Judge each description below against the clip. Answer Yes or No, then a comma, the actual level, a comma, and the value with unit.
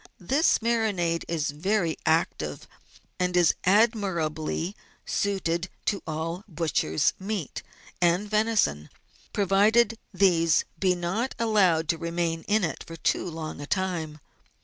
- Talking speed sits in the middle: No, slow, 120 wpm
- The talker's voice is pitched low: No, medium, 175 Hz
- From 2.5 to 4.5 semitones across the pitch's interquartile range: Yes, average, 4.0 semitones